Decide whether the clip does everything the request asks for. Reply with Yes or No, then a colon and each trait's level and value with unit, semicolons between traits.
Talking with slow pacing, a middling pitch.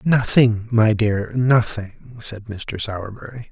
No: slow, 120 wpm; low, 110 Hz